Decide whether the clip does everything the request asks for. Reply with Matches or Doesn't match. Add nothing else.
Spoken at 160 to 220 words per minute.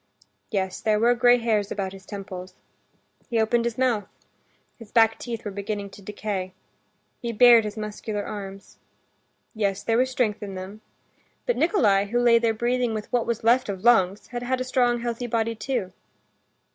Matches